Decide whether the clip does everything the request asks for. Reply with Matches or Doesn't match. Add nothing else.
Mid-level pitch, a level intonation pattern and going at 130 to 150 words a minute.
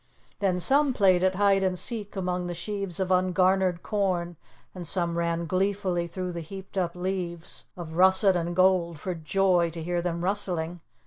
Doesn't match